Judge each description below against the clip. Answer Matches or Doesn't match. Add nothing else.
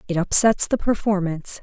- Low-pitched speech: Doesn't match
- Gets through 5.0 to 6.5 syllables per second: Matches